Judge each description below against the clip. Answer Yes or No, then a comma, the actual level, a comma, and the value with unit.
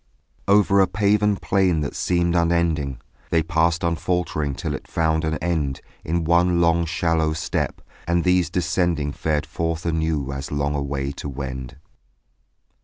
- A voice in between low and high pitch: No, very low, 80 Hz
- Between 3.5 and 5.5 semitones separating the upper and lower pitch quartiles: No, average, 2.8 semitones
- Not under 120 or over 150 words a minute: Yes, average, 145 wpm